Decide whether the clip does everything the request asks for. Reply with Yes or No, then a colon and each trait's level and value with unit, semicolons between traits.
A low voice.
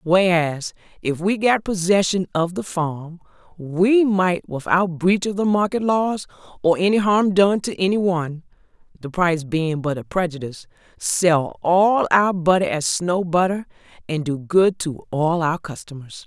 No: medium, 175 Hz